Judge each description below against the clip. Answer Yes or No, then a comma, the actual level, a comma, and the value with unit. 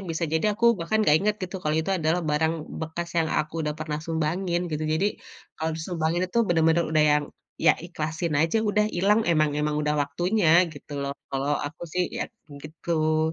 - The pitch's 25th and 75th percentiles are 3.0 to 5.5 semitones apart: No, narrow, 2.5 semitones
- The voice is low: No, medium, 160 Hz